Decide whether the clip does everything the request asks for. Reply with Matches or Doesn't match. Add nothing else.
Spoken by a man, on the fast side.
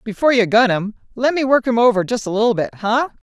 Doesn't match